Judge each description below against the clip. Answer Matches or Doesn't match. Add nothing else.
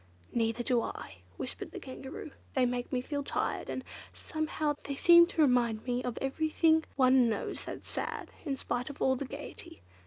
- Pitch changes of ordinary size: Matches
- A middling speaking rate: Matches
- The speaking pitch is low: Doesn't match